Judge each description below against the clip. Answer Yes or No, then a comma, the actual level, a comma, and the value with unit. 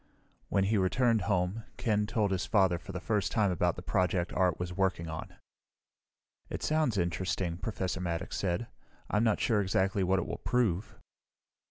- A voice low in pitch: Yes, very low, 95 Hz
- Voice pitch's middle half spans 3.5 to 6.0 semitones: No, average, 2.9 semitones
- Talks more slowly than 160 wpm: No, average, 170 wpm